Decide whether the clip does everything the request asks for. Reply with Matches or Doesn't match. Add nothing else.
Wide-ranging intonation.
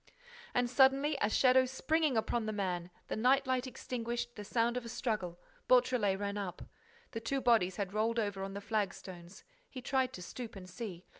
Doesn't match